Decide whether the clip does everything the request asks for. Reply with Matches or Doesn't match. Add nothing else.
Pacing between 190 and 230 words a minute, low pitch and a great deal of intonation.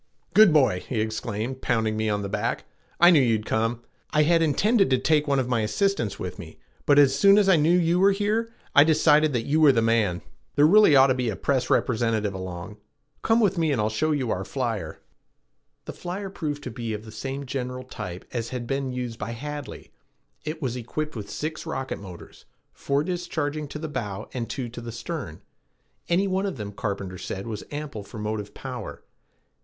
Matches